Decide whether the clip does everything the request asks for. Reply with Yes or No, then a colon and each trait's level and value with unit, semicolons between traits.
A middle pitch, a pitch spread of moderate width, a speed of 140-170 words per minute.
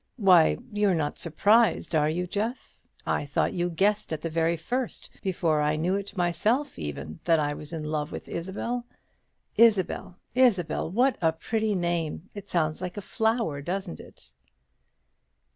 Yes: medium, 175 Hz; average, 4.6 semitones; average, 160 wpm